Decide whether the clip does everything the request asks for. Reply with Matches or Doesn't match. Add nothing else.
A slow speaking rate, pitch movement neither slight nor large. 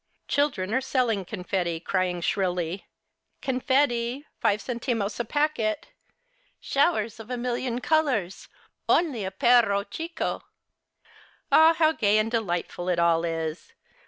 Doesn't match